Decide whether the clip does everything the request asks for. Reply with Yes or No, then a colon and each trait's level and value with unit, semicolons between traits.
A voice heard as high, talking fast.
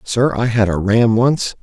No: low, 115 Hz; fast, 220 wpm